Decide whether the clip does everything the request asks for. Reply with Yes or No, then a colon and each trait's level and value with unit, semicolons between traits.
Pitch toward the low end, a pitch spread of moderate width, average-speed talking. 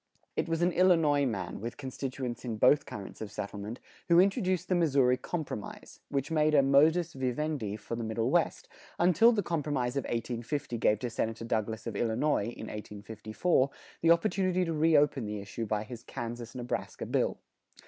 No: low, 130 Hz; wide, 6.2 semitones; average, 170 wpm